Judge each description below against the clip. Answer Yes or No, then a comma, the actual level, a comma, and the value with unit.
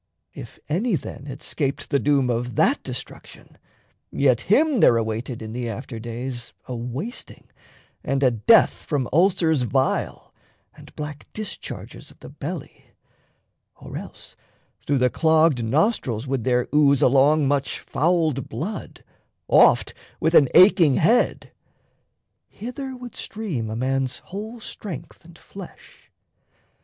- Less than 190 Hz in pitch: Yes, medium, 140 Hz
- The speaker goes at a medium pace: No, slow, 130 wpm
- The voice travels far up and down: Yes, wide, 5.7 semitones